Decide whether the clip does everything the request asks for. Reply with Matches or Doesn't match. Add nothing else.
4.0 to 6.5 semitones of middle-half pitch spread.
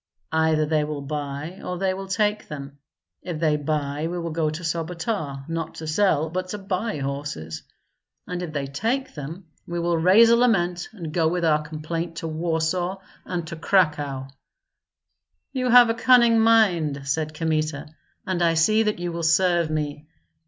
Doesn't match